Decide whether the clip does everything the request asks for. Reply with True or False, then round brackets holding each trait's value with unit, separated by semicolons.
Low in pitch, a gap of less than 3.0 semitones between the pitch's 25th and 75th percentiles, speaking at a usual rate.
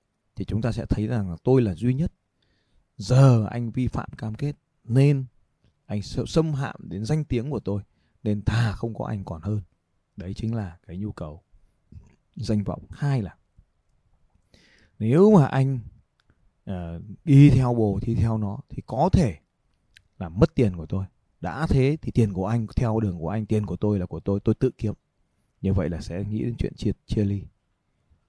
False (110 Hz; 4.5 semitones; 195 wpm)